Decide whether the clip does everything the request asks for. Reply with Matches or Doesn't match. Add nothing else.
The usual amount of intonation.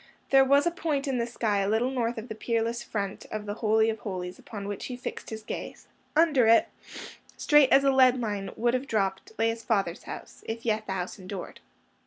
Matches